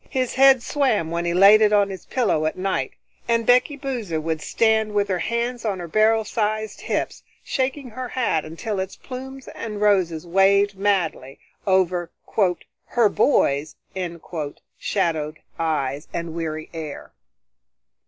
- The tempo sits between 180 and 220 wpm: No, average, 145 wpm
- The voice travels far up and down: Yes, wide, 5.8 semitones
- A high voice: Yes, high, 200 Hz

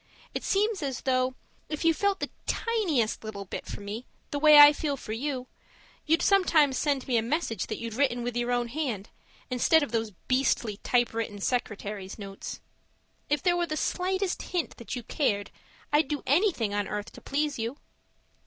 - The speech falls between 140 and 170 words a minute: No, average, 180 wpm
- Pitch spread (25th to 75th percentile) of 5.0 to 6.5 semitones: Yes, wide, 5.4 semitones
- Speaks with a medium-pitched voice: No, very high, 260 Hz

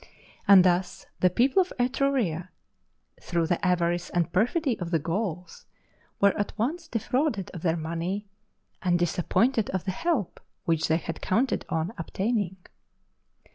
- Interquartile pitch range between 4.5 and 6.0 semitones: Yes, average, 5.2 semitones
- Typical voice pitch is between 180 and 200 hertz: Yes, medium, 185 Hz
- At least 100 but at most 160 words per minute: Yes, average, 140 wpm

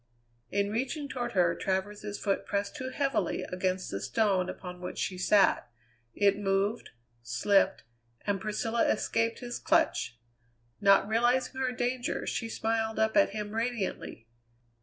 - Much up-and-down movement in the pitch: No, average, 3.7 semitones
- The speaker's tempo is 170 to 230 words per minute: No, average, 140 wpm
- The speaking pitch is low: No, high, 210 Hz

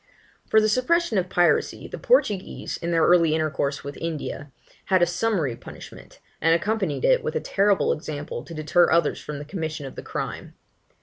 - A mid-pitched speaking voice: Yes, medium, 170 Hz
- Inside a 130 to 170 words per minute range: No, average, 180 wpm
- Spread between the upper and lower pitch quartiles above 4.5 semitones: Yes, average, 5.2 semitones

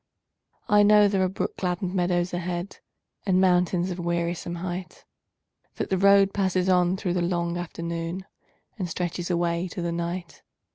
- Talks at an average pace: Yes, average, 155 wpm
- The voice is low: No, medium, 180 Hz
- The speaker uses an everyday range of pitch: No, narrow, 1.4 semitones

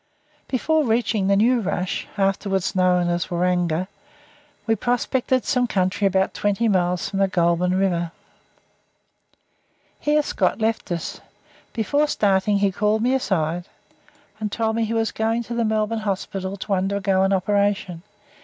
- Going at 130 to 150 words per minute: Yes, average, 145 wpm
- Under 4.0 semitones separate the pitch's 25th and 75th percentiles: Yes, average, 3.4 semitones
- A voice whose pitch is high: Yes, high, 200 Hz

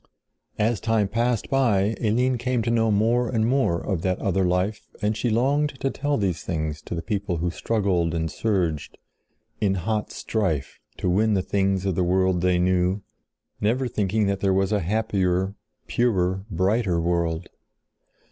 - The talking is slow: No, average, 165 wpm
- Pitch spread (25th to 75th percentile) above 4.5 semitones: No, average, 3.8 semitones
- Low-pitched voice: Yes, low, 100 Hz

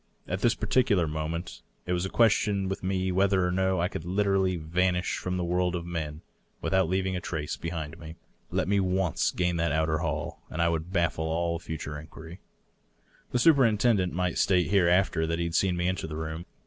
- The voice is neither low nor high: No, very low, 90 Hz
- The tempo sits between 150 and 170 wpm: No, average, 200 wpm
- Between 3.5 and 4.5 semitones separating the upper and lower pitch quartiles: No, narrow, 2.5 semitones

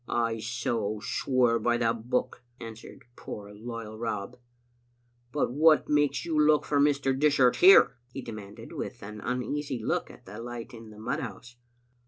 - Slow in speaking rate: No, average, 170 wpm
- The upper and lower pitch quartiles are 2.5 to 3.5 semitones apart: Yes, average, 3.1 semitones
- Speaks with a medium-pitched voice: No, low, 120 Hz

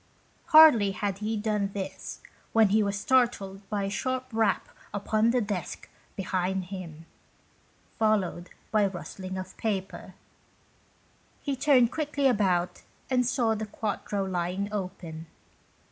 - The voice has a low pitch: No, high, 205 Hz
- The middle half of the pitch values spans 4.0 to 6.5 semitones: No, average, 3.0 semitones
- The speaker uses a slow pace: Yes, slow, 130 wpm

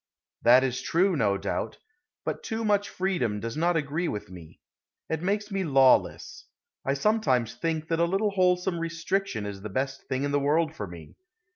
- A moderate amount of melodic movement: No, wide, 6.5 semitones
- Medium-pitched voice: Yes, medium, 160 Hz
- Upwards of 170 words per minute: Yes, average, 180 wpm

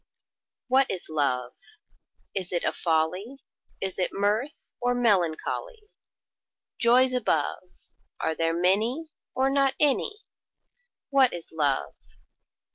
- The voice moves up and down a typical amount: No, wide, 8.0 semitones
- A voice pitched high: Yes, high, 205 Hz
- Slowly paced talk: Yes, slow, 110 wpm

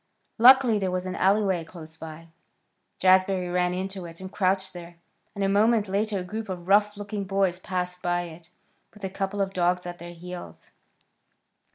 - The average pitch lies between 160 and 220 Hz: Yes, medium, 185 Hz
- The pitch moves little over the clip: Yes, narrow, 2.1 semitones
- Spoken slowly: No, average, 180 wpm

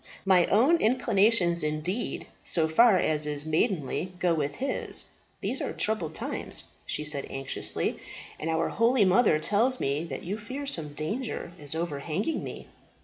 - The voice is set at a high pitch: No, medium, 175 Hz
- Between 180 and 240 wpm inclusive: No, average, 150 wpm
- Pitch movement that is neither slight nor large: No, wide, 6.3 semitones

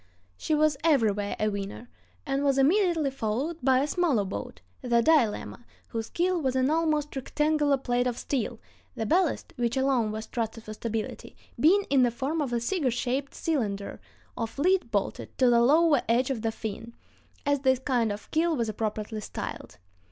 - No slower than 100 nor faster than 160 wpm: No, average, 175 wpm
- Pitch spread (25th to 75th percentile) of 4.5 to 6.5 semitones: Yes, average, 4.8 semitones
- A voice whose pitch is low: No, very high, 255 Hz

